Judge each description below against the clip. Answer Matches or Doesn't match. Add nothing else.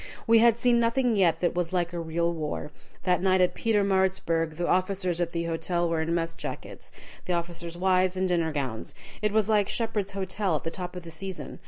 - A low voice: Doesn't match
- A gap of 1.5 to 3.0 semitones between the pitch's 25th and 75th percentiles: Matches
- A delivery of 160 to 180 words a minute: Doesn't match